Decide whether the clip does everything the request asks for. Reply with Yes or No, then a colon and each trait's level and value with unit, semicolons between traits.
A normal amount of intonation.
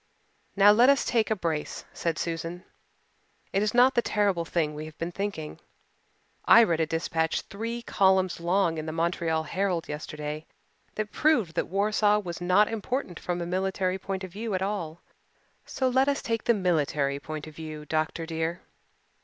Yes: average, 4.3 semitones